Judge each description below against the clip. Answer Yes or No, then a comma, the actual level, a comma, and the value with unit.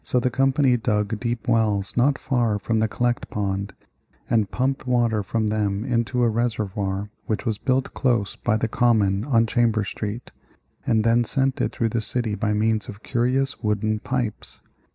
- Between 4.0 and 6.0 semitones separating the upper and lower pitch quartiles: No, narrow, 2.6 semitones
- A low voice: Yes, low, 115 Hz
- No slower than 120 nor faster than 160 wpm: No, average, 175 wpm